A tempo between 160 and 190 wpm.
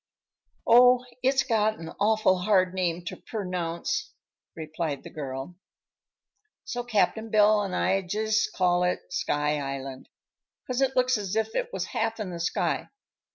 No: average, 150 wpm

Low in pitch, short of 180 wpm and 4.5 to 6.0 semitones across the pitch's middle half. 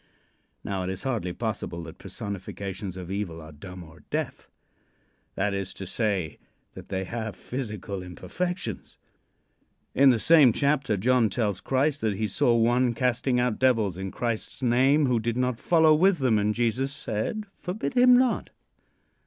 Yes: low, 115 Hz; average, 160 wpm; average, 5.3 semitones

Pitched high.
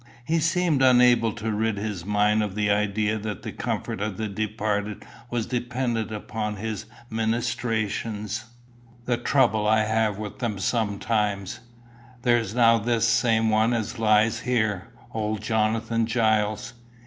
No: low, 110 Hz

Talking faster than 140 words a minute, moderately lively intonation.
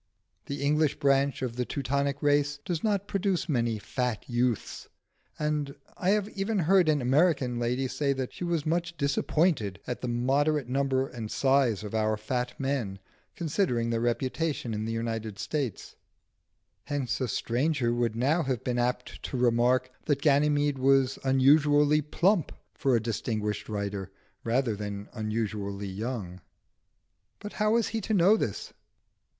Yes: average, 150 wpm; average, 4.4 semitones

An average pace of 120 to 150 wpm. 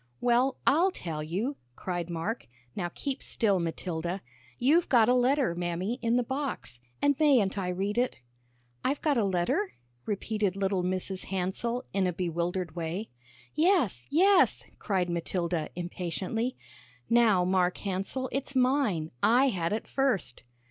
Yes: average, 140 wpm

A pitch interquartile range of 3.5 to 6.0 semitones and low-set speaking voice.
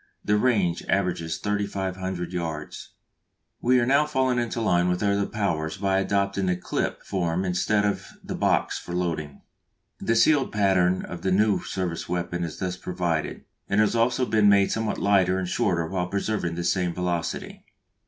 No: average, 2.9 semitones; very low, 95 Hz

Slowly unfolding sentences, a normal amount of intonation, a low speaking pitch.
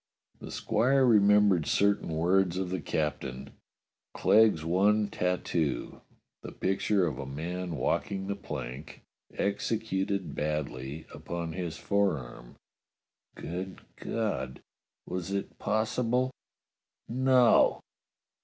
Yes: slow, 100 wpm; average, 4.7 semitones; very low, 95 Hz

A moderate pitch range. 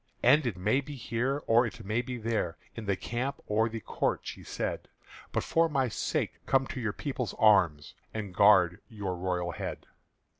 Yes: average, 4.3 semitones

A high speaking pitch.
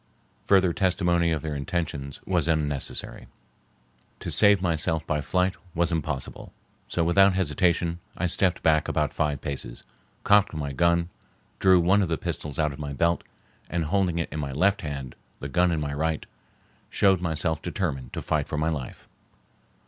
No: very low, 80 Hz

